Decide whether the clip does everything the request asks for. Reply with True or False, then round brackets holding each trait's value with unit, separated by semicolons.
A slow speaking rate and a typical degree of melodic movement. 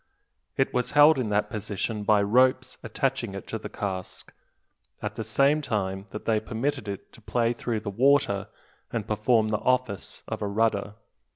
False (175 wpm; 3.7 semitones)